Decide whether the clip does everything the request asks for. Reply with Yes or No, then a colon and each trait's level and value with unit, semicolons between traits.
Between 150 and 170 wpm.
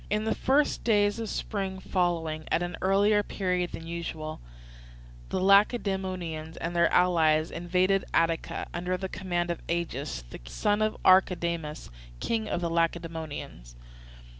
No: average, 140 wpm